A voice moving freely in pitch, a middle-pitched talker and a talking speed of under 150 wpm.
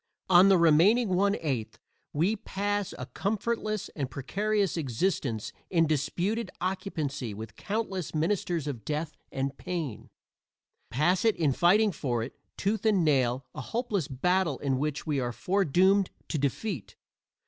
Yes: wide, 6.3 semitones; medium, 170 Hz; average, 140 wpm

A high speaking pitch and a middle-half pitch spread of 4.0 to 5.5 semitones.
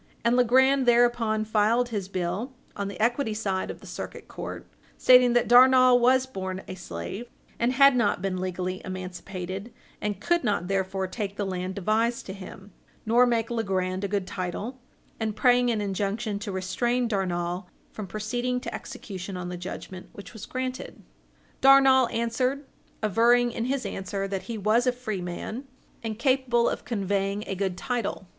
Yes: high, 215 Hz; average, 4.3 semitones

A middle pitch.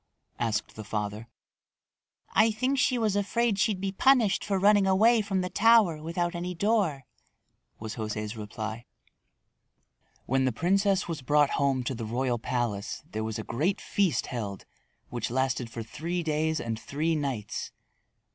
Yes: medium, 150 Hz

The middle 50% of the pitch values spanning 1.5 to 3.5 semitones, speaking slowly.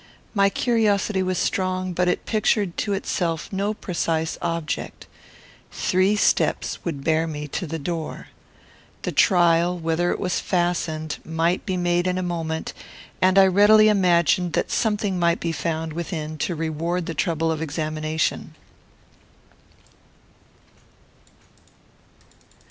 Yes: narrow, 2.5 semitones; slow, 125 wpm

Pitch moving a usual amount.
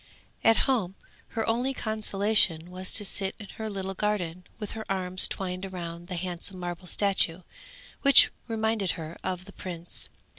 Yes: average, 3.1 semitones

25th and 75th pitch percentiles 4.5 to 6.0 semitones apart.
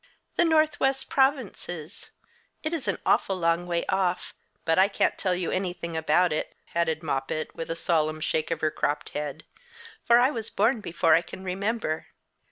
Yes: wide, 5.4 semitones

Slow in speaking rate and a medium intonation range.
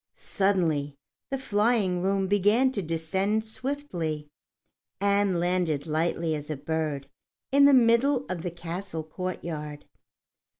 Yes: slow, 120 wpm; average, 4.6 semitones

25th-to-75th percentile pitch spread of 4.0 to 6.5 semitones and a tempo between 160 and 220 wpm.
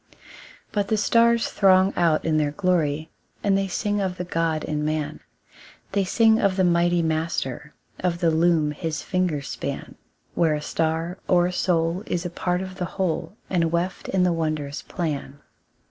No: average, 2.9 semitones; average, 175 wpm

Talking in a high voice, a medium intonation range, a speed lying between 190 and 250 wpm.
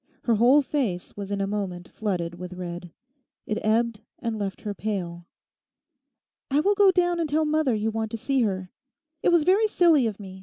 No: high, 220 Hz; wide, 7.6 semitones; average, 195 wpm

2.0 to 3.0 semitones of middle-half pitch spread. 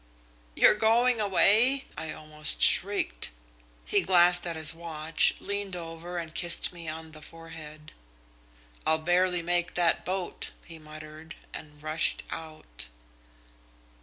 Yes: narrow, 2.5 semitones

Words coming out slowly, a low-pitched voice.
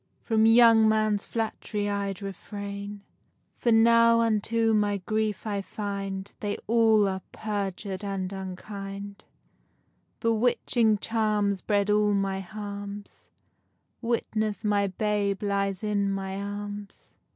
No: slow, 110 wpm; high, 205 Hz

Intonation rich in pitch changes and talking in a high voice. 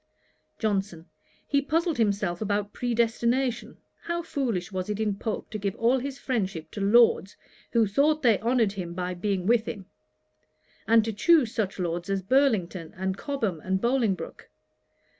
No: average, 4.3 semitones; high, 215 Hz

